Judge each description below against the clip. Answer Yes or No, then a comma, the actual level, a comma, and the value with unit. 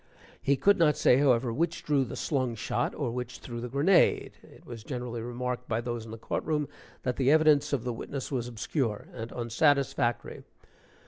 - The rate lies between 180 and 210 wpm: Yes, average, 190 wpm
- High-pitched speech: No, low, 125 Hz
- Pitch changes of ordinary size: Yes, average, 3.2 semitones